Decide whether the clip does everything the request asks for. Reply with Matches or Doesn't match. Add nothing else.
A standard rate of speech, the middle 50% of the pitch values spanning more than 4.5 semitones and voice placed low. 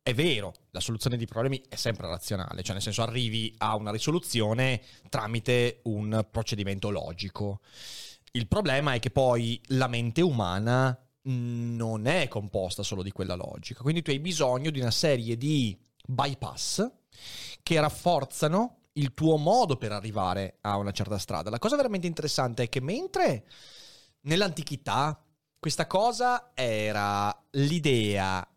Matches